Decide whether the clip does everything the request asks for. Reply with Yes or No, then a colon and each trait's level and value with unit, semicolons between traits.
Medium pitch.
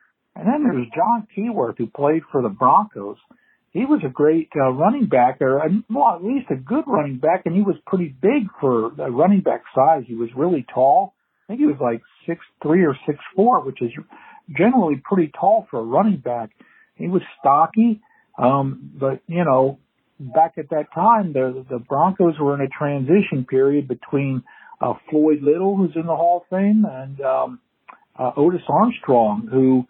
Yes: medium, 160 Hz